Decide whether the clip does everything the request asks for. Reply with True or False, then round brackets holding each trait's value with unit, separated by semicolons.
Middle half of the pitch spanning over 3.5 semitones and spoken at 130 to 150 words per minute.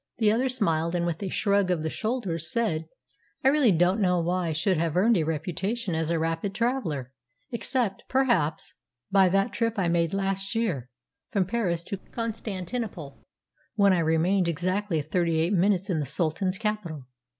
False (4.3 semitones; 170 wpm)